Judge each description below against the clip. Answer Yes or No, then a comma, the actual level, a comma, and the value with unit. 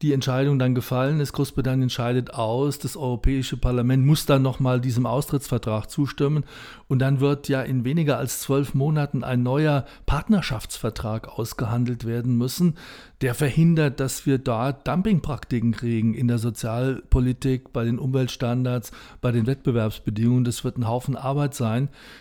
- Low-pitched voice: Yes, low, 130 Hz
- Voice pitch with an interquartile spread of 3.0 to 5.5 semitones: No, narrow, 2.6 semitones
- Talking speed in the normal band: Yes, average, 145 wpm